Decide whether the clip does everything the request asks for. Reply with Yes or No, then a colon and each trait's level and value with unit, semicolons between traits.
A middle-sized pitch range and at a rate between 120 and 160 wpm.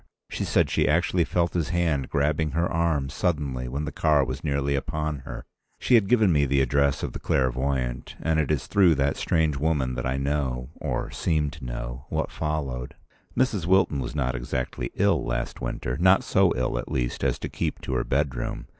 No: average, 3.7 semitones; average, 190 wpm